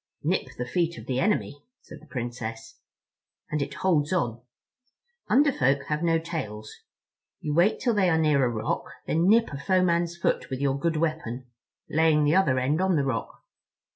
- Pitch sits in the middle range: Yes, medium, 150 Hz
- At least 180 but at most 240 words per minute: Yes, average, 185 wpm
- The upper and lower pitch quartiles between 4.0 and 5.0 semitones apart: Yes, average, 4.7 semitones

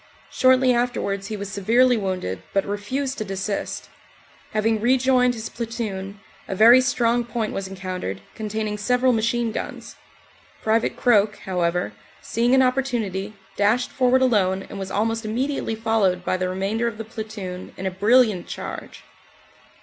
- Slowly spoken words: No, average, 145 wpm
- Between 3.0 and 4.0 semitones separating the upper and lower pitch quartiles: Yes, average, 3.7 semitones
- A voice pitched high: Yes, high, 220 Hz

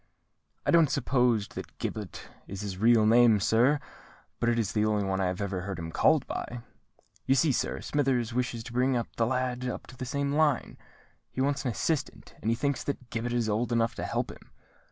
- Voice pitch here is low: Yes, low, 120 Hz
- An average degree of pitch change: Yes, average, 3.3 semitones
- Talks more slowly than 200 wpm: No, fast, 205 wpm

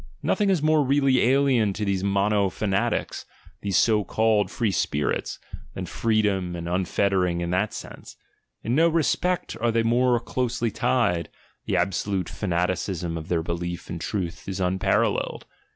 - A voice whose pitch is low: Yes, low, 100 Hz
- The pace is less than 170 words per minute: Yes, average, 150 wpm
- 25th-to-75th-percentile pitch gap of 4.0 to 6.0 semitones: Yes, average, 4.7 semitones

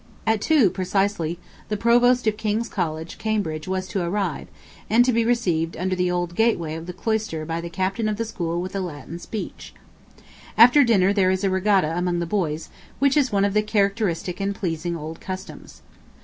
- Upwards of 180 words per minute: Yes, average, 190 wpm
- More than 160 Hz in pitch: Yes, high, 190 Hz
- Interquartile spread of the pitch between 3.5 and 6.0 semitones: Yes, average, 4.0 semitones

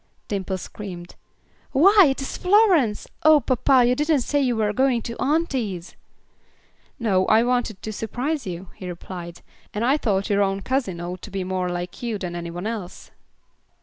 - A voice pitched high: Yes, high, 220 Hz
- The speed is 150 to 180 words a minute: Yes, average, 175 wpm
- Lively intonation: Yes, wide, 6.1 semitones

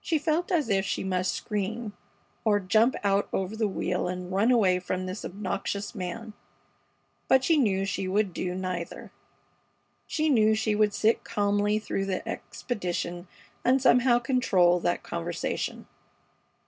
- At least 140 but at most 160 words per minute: Yes, average, 145 wpm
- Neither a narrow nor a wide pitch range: Yes, average, 3.8 semitones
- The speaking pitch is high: Yes, high, 205 Hz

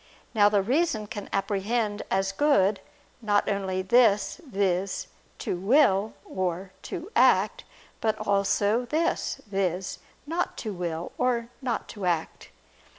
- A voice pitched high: Yes, high, 205 Hz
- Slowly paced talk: Yes, slow, 125 wpm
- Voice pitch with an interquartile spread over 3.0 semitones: Yes, average, 3.7 semitones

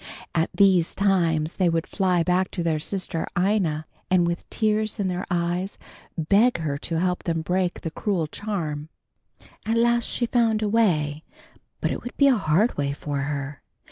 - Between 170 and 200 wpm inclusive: Yes, average, 175 wpm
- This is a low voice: No, medium, 180 Hz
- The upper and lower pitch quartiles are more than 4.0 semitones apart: Yes, average, 4.4 semitones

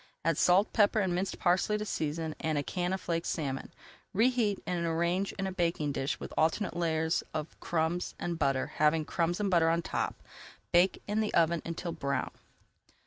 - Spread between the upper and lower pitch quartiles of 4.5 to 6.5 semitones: No, average, 3.0 semitones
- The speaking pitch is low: No, medium, 170 Hz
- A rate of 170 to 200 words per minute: Yes, average, 195 wpm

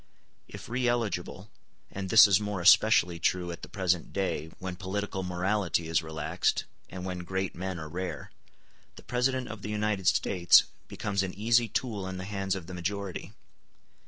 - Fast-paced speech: No, average, 170 wpm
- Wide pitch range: No, narrow, 2.6 semitones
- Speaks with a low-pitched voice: Yes, very low, 95 Hz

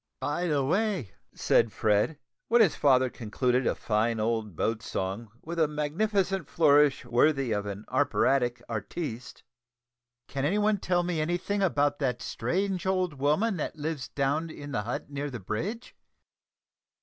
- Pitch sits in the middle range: Yes, medium, 145 Hz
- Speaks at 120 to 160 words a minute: Yes, average, 155 wpm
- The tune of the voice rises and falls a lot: Yes, wide, 6.6 semitones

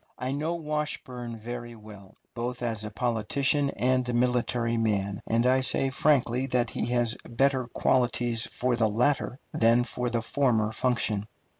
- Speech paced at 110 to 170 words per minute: Yes, average, 155 wpm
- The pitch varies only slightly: Yes, narrow, 2.0 semitones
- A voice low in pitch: Yes, low, 120 Hz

